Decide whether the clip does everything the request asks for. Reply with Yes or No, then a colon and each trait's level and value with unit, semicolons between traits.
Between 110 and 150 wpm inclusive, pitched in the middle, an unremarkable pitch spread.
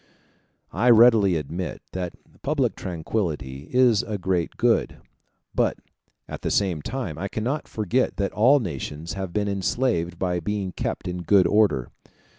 No: average, 145 wpm; very low, 95 Hz; average, 4.7 semitones